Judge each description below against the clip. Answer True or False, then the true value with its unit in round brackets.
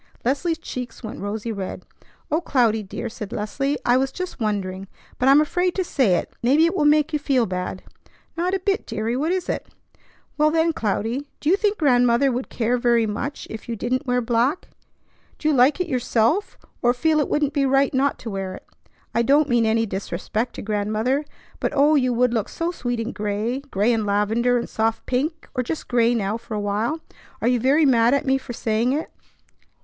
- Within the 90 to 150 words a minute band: False (205 wpm)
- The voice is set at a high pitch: True (245 Hz)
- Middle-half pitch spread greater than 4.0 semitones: True (4.6 semitones)